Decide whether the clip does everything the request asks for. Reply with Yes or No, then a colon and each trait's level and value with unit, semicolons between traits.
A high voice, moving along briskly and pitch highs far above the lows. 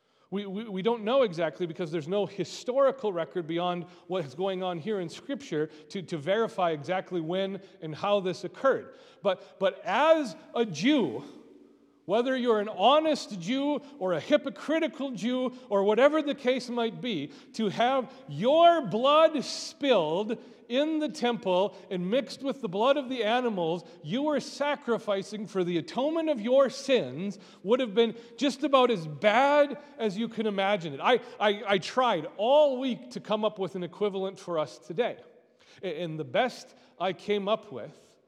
No: high, 220 Hz; average, 170 wpm; wide, 5.8 semitones